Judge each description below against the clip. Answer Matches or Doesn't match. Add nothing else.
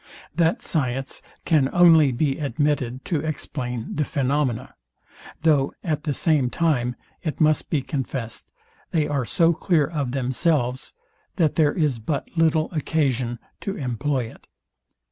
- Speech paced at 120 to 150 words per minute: Matches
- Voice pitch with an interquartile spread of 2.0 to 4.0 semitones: Matches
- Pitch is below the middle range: Doesn't match